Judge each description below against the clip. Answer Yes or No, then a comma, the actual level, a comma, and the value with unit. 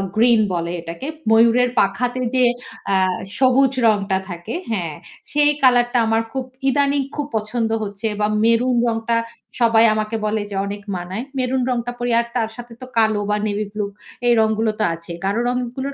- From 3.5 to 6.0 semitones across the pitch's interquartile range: No, average, 3.0 semitones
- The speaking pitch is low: No, high, 225 Hz